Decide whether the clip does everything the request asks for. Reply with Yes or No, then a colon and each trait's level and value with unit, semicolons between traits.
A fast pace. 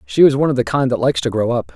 Yes: fast, 375 wpm